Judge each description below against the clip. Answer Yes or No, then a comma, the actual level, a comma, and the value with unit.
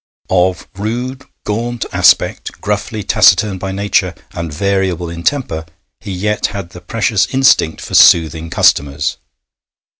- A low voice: Yes, very low, 95 Hz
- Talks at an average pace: No, slow, 125 wpm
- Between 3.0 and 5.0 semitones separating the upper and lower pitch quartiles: Yes, average, 4.1 semitones